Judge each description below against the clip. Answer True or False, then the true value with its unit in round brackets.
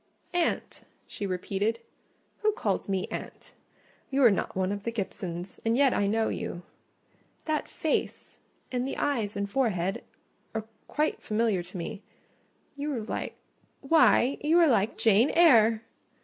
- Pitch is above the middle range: True (225 Hz)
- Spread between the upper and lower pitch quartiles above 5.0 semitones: True (5.6 semitones)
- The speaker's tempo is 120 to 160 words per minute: True (140 wpm)